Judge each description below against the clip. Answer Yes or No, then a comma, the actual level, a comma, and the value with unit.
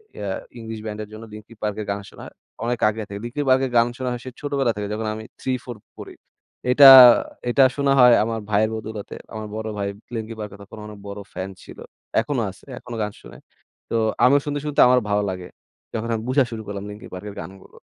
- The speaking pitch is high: No, low, 110 Hz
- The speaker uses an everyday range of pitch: Yes, average, 3.1 semitones